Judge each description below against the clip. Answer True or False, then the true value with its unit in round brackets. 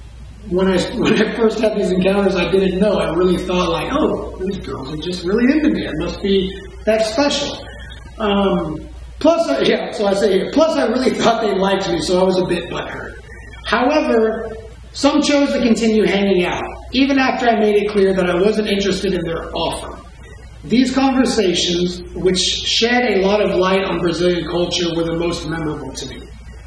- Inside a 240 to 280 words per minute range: False (190 wpm)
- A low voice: False (195 Hz)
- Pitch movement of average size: True (3.9 semitones)